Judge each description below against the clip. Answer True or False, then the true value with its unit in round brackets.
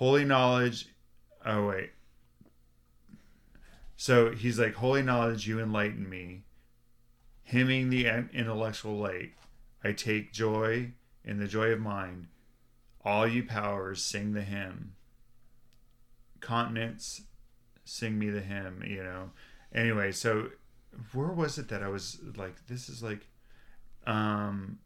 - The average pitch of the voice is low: True (115 Hz)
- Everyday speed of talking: False (120 wpm)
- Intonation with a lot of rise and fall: False (2.9 semitones)